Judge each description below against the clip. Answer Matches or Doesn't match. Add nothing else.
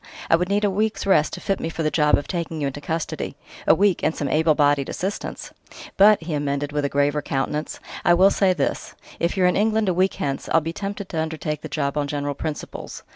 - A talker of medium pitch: Matches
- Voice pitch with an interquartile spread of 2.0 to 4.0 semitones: Doesn't match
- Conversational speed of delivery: Doesn't match